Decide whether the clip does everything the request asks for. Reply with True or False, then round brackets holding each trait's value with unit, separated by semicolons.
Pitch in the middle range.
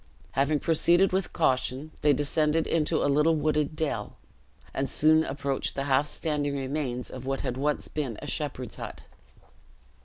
True (145 Hz)